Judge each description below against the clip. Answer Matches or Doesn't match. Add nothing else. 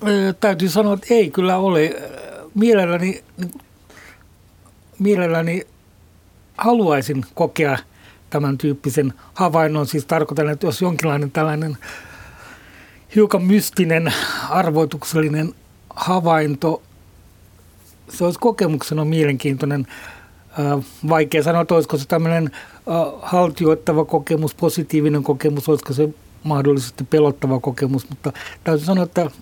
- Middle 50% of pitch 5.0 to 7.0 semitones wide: Doesn't match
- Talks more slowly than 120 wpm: Matches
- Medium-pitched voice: Matches